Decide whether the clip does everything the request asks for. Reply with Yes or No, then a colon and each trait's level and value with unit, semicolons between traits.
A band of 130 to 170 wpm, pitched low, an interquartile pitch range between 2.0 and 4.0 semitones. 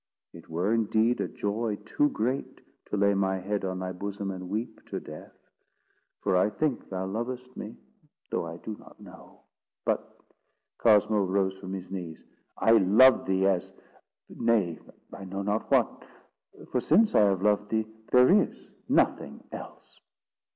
Yes: average, 150 wpm; low, 100 Hz; average, 2.9 semitones